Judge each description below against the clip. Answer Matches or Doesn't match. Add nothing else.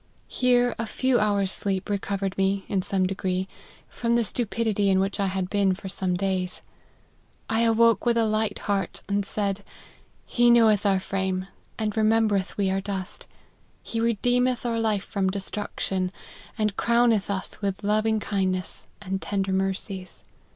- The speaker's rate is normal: Matches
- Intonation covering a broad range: Doesn't match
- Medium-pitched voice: Doesn't match